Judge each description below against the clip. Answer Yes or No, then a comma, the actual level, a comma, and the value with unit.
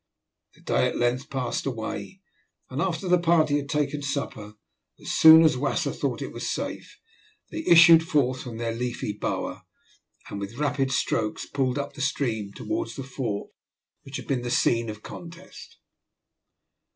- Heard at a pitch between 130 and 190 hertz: Yes, low, 135 Hz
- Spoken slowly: No, average, 165 wpm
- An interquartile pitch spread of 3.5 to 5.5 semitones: Yes, average, 4.9 semitones